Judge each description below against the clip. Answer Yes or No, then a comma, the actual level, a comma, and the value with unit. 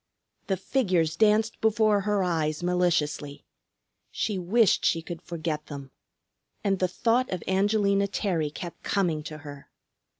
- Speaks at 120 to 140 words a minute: Yes, slow, 135 wpm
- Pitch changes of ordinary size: Yes, average, 4.6 semitones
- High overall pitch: No, medium, 180 Hz